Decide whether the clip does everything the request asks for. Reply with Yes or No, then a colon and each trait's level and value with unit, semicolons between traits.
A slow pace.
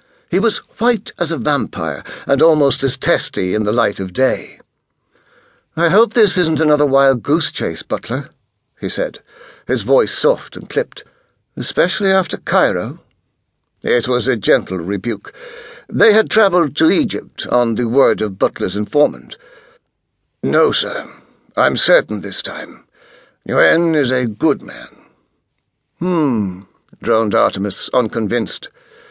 Yes: slow, 130 wpm